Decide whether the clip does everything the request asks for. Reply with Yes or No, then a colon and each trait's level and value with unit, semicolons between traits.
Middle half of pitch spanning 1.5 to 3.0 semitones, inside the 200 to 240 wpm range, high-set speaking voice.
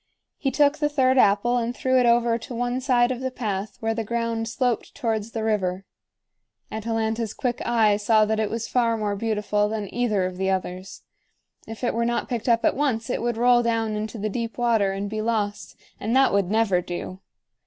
Yes: narrow, 2.4 semitones; fast, 205 wpm; high, 225 Hz